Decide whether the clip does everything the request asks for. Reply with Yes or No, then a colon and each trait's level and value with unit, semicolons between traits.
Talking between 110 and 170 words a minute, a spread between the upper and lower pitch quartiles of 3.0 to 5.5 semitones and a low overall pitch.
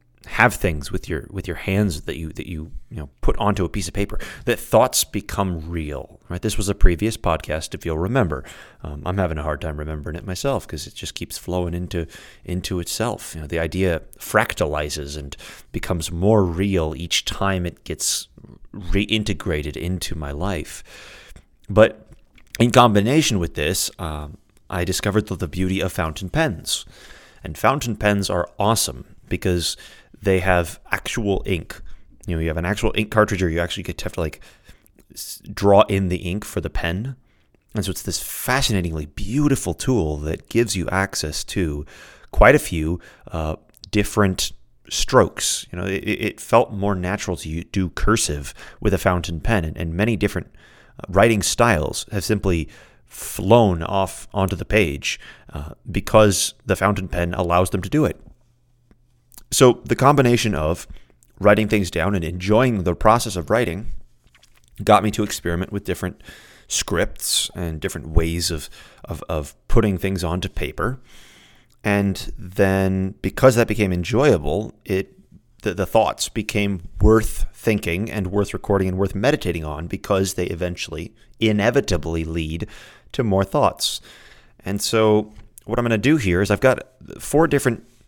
Yes: average, 165 wpm; average, 4.3 semitones; very low, 95 Hz